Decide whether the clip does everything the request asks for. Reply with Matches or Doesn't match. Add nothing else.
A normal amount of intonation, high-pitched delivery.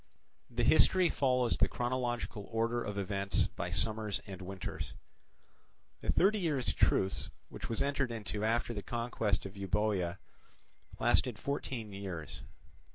Doesn't match